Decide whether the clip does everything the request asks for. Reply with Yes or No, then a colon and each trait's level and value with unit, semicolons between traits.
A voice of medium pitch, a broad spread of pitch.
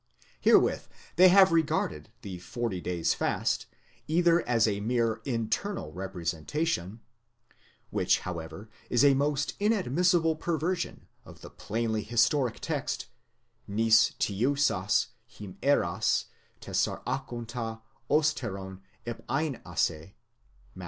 No: low, 115 Hz; wide, 7.4 semitones